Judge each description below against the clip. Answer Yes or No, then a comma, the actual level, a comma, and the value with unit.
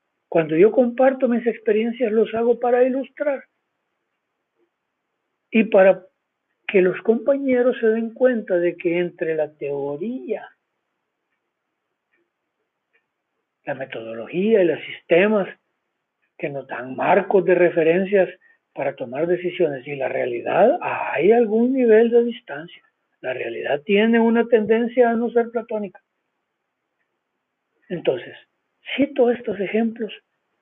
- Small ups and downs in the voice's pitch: No, average, 5.2 semitones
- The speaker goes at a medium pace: No, slow, 115 wpm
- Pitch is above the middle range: Yes, high, 220 Hz